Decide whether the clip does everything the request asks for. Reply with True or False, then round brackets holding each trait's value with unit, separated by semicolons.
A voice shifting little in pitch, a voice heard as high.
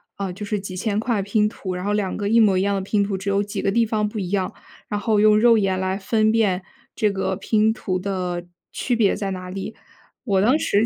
True (2.1 semitones; 200 Hz)